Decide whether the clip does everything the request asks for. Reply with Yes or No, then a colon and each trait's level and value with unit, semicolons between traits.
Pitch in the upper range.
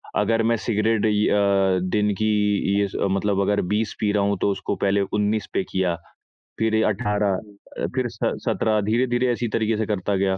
No: low, 105 Hz